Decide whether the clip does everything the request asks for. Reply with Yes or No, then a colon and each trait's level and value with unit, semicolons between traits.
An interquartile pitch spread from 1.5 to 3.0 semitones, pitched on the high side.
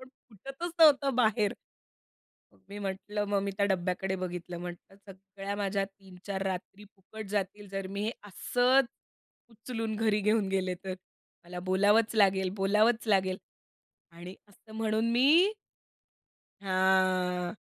Yes: narrow, 2.6 semitones; high, 200 Hz